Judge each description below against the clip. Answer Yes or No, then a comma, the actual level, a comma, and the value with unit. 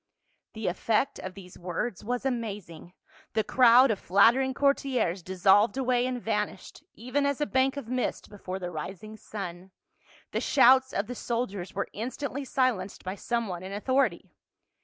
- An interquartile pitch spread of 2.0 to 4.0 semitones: No, average, 5.1 semitones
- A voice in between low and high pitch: No, high, 225 Hz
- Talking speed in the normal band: Yes, average, 160 wpm